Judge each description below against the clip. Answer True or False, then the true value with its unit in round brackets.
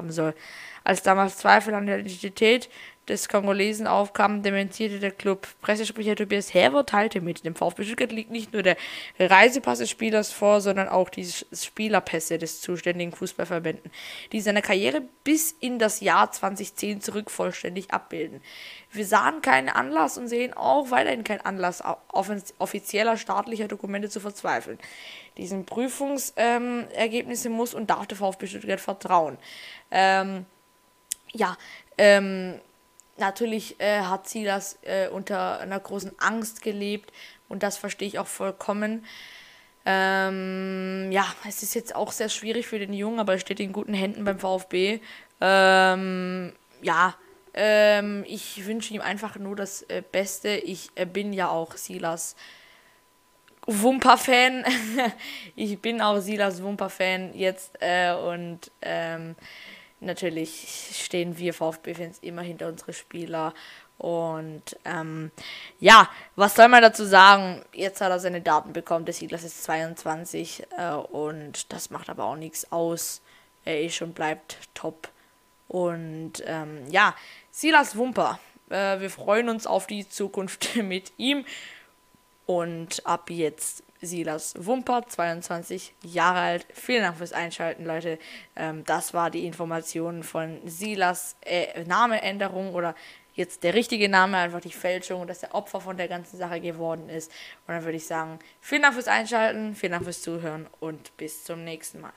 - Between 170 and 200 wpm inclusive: False (145 wpm)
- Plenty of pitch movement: False (3.6 semitones)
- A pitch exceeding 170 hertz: True (190 Hz)